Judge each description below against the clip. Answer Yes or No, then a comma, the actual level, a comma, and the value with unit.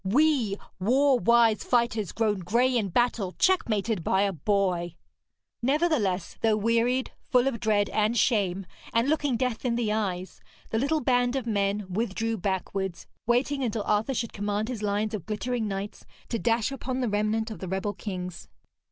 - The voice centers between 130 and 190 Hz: No, high, 220 Hz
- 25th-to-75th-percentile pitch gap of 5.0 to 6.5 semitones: No, average, 3.4 semitones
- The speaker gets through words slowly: No, average, 165 wpm